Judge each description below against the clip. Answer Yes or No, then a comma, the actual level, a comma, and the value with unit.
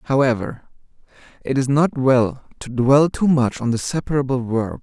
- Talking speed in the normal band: Yes, average, 160 wpm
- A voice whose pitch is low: Yes, low, 130 Hz